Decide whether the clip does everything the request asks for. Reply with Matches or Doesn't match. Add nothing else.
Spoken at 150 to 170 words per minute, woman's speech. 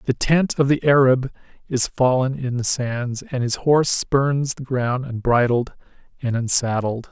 Doesn't match